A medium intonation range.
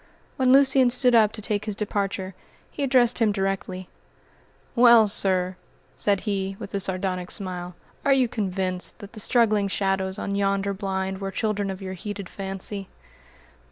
No: narrow, 2.2 semitones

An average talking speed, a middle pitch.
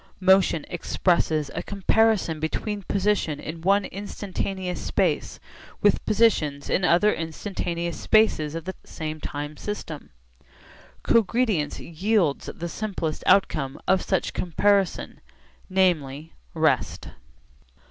No: slow, 105 wpm; medium, 180 Hz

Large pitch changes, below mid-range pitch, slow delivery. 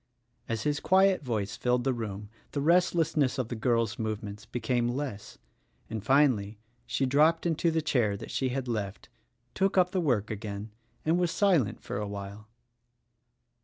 No: wide, 6.3 semitones; low, 125 Hz; average, 165 wpm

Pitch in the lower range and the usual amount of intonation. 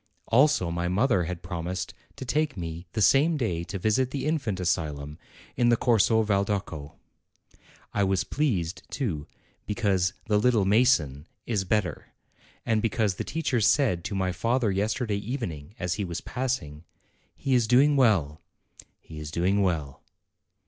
No: low, 100 Hz; wide, 5.7 semitones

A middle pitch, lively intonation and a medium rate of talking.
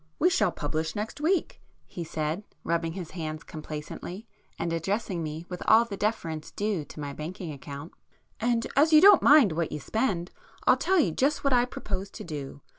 Yes: medium, 180 Hz; wide, 6.5 semitones; average, 180 wpm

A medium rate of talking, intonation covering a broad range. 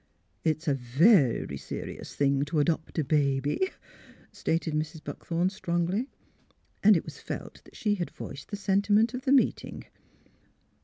Yes: average, 165 wpm; wide, 5.8 semitones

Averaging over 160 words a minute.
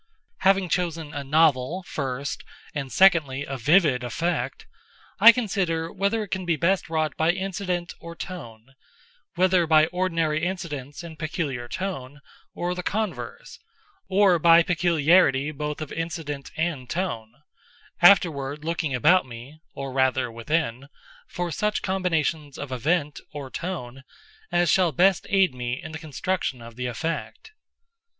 No: slow, 135 wpm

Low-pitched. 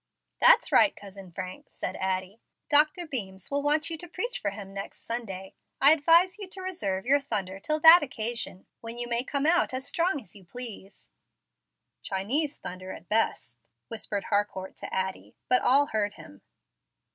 No: high, 230 Hz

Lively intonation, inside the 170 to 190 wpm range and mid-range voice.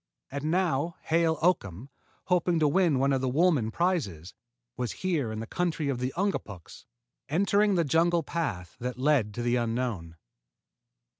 No: wide, 6.1 semitones; average, 155 wpm; medium, 145 Hz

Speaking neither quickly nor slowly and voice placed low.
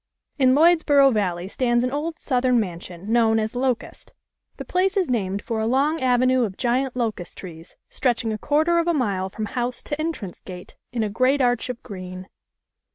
No: average, 195 wpm; high, 245 Hz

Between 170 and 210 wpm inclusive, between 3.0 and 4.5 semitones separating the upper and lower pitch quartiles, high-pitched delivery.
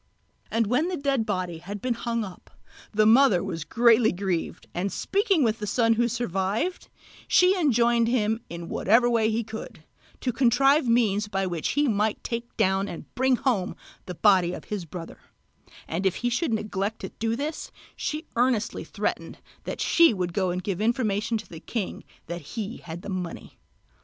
Yes: average, 180 wpm; average, 4.1 semitones; high, 220 Hz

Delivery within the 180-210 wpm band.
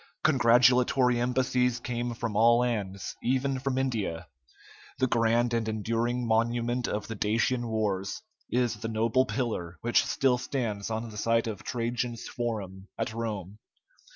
No: average, 140 wpm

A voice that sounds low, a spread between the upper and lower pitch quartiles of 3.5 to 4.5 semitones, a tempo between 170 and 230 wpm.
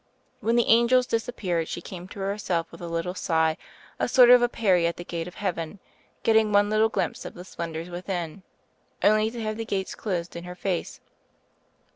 No: high, 190 Hz; average, 4.2 semitones; average, 200 wpm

